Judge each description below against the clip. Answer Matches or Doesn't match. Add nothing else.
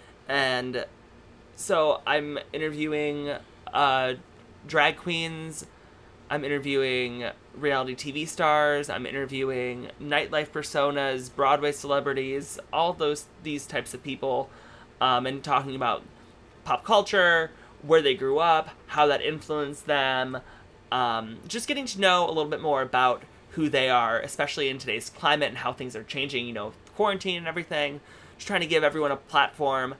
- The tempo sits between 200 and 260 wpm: Doesn't match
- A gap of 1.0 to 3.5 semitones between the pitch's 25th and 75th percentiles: Matches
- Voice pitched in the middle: Matches